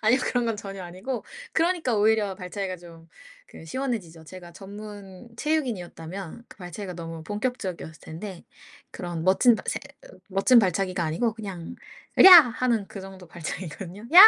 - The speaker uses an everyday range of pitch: Yes, average, 4.5 semitones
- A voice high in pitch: Yes, high, 195 Hz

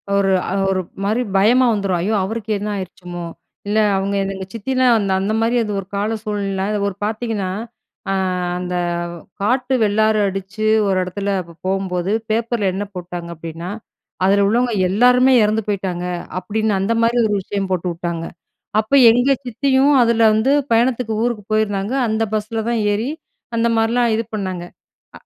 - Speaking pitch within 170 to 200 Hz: No, high, 210 Hz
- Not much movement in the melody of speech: No, average, 3.0 semitones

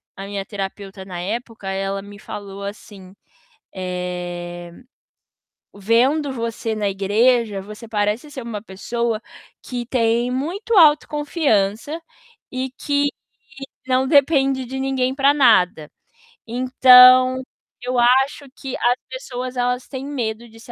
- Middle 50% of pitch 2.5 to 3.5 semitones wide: No, average, 4.6 semitones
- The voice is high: Yes, high, 235 Hz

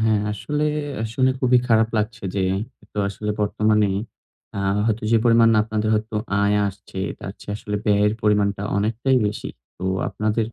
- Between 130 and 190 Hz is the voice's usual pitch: No, low, 105 Hz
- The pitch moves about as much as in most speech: No, narrow, 1.6 semitones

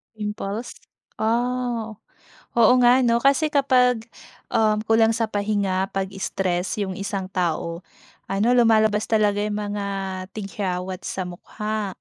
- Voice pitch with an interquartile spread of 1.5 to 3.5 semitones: Yes, average, 2.8 semitones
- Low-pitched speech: No, high, 210 Hz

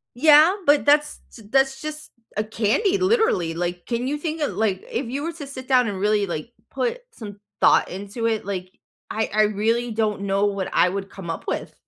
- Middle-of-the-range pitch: No, high, 225 Hz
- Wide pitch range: Yes, wide, 6.5 semitones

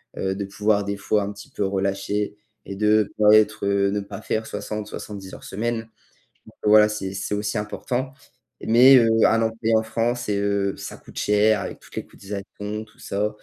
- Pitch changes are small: Yes, narrow, 1.5 semitones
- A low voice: Yes, low, 105 Hz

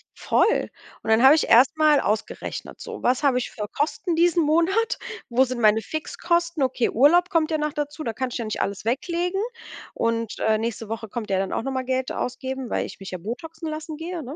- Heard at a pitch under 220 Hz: No, very high, 265 Hz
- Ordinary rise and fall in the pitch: No, wide, 5.7 semitones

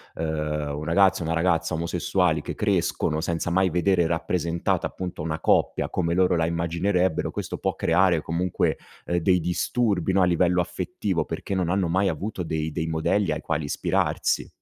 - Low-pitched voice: Yes, very low, 85 Hz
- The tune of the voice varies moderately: No, narrow, 2.3 semitones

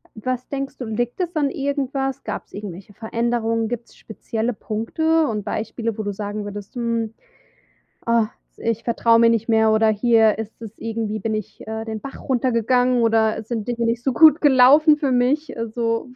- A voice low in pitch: No, high, 230 Hz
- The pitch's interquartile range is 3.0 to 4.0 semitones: No, narrow, 2.4 semitones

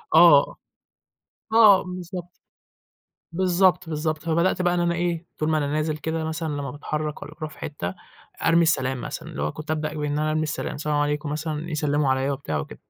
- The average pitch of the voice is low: No, medium, 155 Hz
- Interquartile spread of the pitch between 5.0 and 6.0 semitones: No, narrow, 2.4 semitones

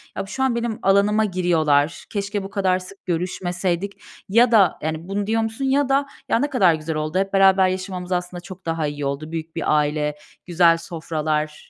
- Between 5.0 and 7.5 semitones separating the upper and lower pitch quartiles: No, average, 3.8 semitones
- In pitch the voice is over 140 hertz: Yes, medium, 185 Hz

